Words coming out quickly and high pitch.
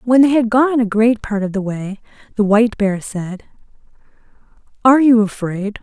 No: average, 175 wpm; high, 220 Hz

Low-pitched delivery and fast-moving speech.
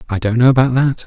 Yes: low, 125 Hz; fast, 280 wpm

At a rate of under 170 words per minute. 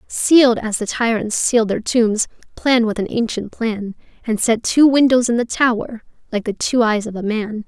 No: fast, 205 wpm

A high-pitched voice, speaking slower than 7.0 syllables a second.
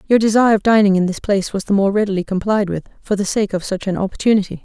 No: high, 200 Hz; 7.2 syllables/s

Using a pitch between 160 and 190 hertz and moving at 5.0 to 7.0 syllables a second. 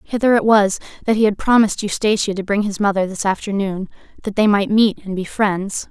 No: high, 205 Hz; 5.7 syllables/s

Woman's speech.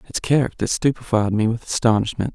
No: male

